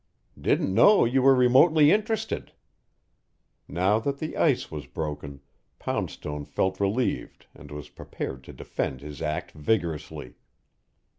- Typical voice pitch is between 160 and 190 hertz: No, very low, 95 Hz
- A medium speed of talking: No, slow, 125 wpm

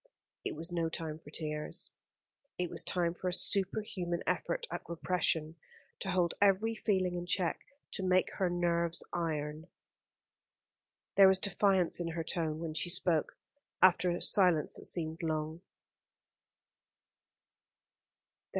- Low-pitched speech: No, medium, 175 Hz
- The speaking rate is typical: No, slow, 130 wpm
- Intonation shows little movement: Yes, narrow, 2.3 semitones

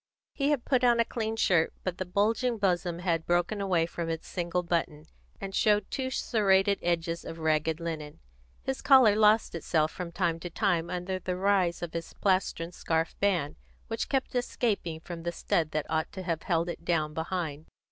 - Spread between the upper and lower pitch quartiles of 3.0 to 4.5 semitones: Yes, average, 3.5 semitones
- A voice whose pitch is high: No, medium, 175 Hz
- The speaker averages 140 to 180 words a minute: No, average, 190 wpm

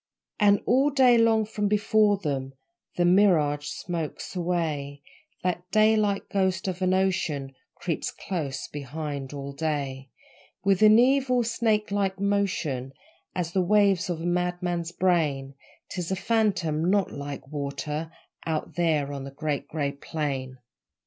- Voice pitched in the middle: Yes, medium, 175 Hz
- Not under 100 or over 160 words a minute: Yes, slow, 135 wpm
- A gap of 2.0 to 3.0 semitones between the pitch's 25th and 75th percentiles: No, wide, 5.5 semitones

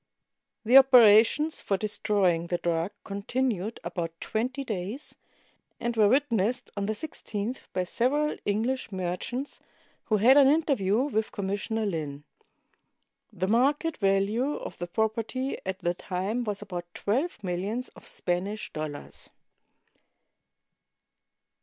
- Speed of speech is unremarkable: No, slow, 120 wpm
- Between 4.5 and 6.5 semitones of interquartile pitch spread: Yes, average, 5.1 semitones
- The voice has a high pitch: Yes, high, 215 Hz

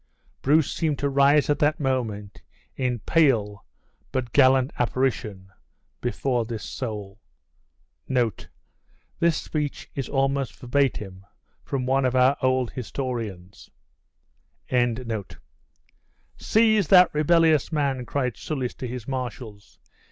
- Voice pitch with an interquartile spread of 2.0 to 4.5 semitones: Yes, average, 3.2 semitones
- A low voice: Yes, low, 130 Hz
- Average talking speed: No, slow, 105 wpm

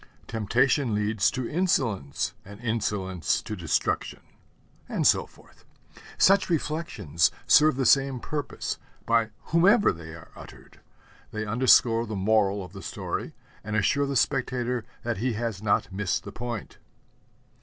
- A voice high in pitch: No, low, 115 Hz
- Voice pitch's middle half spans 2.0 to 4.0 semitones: No, average, 4.6 semitones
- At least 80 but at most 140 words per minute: Yes, slow, 135 wpm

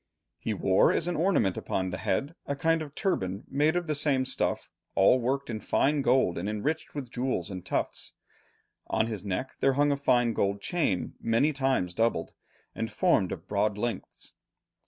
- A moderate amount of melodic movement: No, wide, 6.3 semitones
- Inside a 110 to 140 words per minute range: No, average, 180 wpm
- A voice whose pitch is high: No, low, 125 Hz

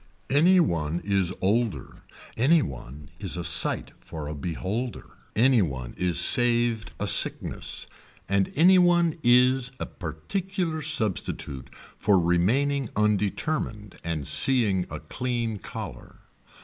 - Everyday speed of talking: No, slow, 120 wpm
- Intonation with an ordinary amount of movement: No, wide, 7.4 semitones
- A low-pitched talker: Yes, low, 105 Hz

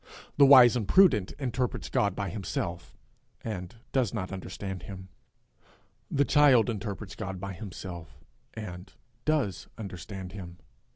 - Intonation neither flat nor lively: Yes, average, 4.4 semitones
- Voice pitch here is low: Yes, low, 100 Hz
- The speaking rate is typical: No, slow, 125 wpm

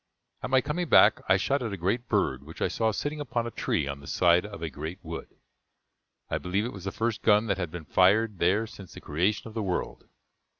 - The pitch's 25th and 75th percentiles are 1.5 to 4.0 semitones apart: No, average, 4.6 semitones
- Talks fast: Yes, fast, 240 wpm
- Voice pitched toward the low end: Yes, low, 100 Hz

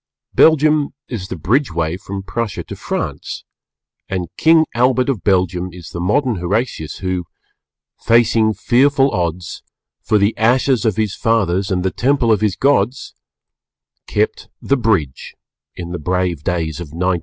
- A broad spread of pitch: Yes, wide, 5.7 semitones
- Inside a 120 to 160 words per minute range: Yes, average, 150 wpm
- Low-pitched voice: Yes, low, 100 Hz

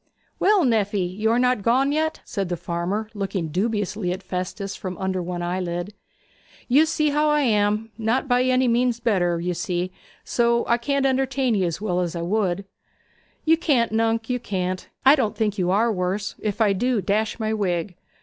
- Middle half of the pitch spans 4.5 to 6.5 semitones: Yes, average, 5.0 semitones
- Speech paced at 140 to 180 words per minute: No, average, 190 wpm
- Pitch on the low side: No, high, 210 Hz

